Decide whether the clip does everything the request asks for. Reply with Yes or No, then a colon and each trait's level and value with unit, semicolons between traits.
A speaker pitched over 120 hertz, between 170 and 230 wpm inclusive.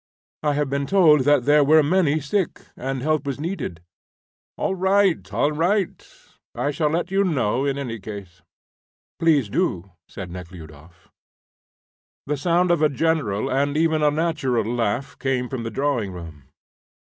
No: medium, 140 Hz; average, 155 wpm